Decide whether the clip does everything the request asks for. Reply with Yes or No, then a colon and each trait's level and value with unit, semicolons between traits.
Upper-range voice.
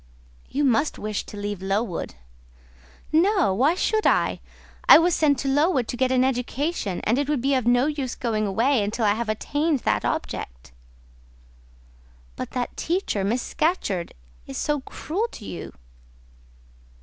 Yes: very high, 255 Hz